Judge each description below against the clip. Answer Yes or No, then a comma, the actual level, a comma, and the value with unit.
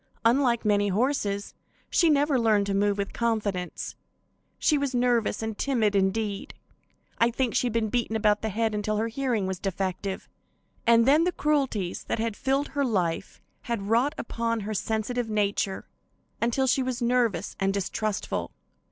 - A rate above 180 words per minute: No, average, 160 wpm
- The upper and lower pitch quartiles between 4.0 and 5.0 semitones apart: No, average, 3.4 semitones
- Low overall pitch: No, high, 225 Hz